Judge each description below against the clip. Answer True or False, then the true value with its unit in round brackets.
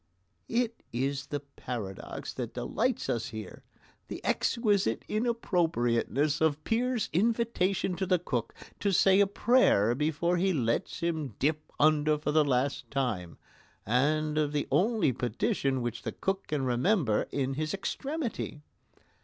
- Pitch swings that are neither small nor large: False (7.0 semitones)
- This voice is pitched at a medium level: True (150 Hz)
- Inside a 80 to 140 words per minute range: True (135 wpm)